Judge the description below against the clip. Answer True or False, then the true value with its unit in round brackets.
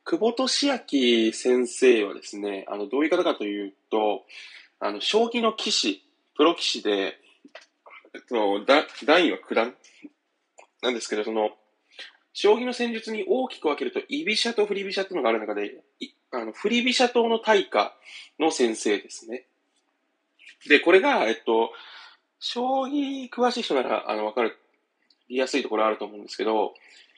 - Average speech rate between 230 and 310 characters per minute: True (300 characters per minute)